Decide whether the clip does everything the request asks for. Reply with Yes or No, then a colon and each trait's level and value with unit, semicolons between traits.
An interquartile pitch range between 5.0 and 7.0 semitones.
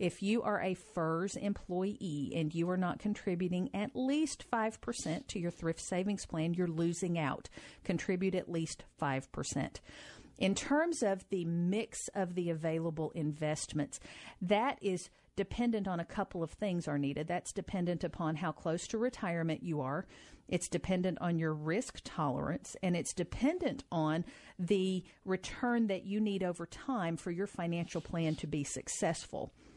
No: average, 3.4 semitones